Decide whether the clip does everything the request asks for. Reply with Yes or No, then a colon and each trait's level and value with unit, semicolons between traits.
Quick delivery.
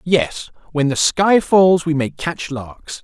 No: average, 180 wpm